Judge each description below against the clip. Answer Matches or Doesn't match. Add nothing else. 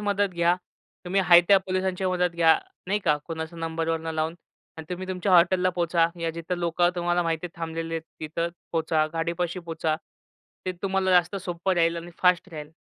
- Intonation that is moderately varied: Doesn't match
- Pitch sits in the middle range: Matches